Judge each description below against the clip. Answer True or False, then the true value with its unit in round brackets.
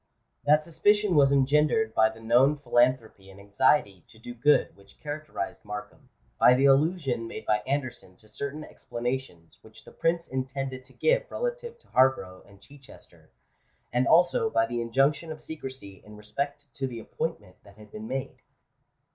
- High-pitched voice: False (130 Hz)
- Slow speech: False (165 wpm)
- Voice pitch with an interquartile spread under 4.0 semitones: False (5.2 semitones)